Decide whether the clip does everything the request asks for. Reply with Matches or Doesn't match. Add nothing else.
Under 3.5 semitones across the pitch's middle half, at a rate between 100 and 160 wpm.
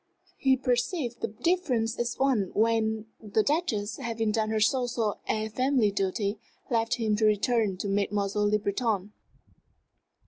Matches